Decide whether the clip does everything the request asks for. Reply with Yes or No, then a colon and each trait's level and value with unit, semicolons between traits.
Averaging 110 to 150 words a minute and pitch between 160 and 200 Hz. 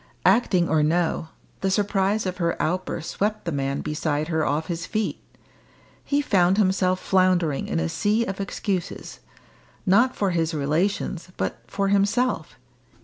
Yes: average, 145 wpm; medium, 185 Hz